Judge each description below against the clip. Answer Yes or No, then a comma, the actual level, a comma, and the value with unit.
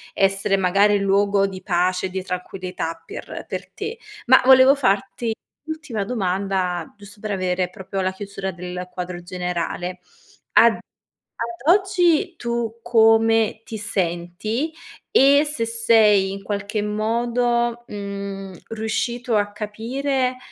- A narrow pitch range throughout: No, average, 3.8 semitones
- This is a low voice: No, high, 205 Hz